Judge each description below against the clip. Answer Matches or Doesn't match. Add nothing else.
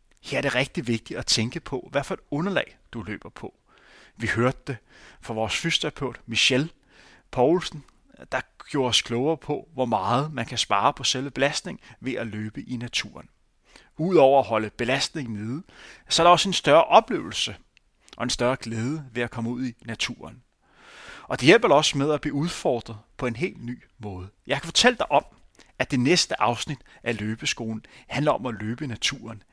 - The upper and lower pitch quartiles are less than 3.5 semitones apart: Doesn't match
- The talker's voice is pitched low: Matches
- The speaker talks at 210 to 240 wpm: Doesn't match